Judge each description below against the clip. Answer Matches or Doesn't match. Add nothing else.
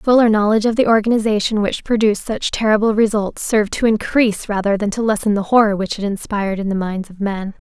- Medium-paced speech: Doesn't match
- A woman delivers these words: Matches